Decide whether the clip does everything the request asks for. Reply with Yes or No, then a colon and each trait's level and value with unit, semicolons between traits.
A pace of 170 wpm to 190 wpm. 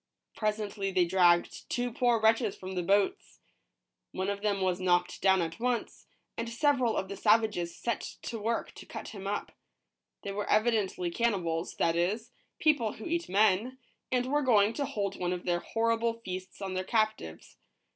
Yes: average, 175 wpm